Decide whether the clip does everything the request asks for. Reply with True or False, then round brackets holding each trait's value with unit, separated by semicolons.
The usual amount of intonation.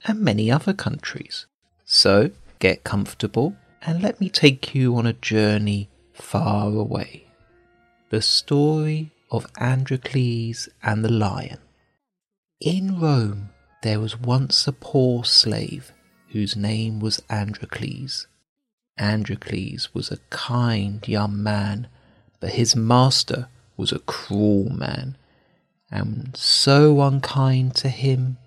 True (4.5 semitones)